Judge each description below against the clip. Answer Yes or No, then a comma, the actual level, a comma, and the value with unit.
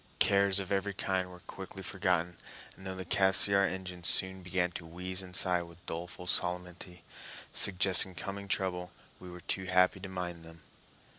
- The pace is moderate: Yes, average, 165 wpm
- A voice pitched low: Yes, very low, 90 Hz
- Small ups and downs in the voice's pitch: Yes, narrow, 1.3 semitones